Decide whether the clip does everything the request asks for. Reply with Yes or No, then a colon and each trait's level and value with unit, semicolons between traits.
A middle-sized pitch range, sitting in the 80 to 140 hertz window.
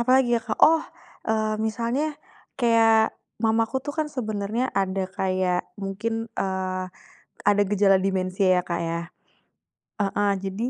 No: average, 3.2 semitones; high, 205 Hz